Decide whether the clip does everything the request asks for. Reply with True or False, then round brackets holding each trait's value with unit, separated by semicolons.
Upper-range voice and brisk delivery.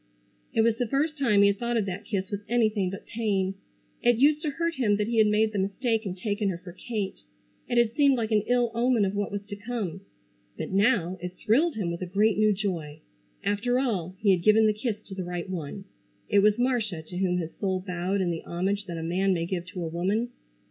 True (205 Hz; 240 wpm)